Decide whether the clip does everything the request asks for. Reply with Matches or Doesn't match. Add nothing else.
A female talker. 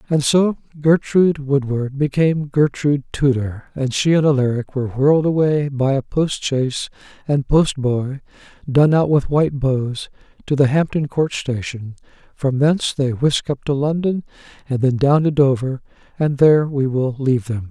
Doesn't match